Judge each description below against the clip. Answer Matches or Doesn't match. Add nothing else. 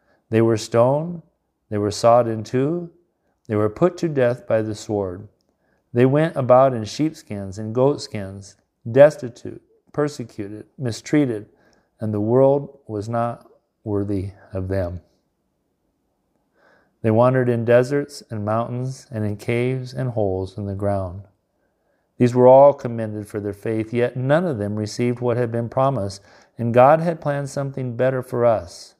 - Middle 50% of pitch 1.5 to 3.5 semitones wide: Doesn't match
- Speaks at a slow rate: Doesn't match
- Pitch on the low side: Matches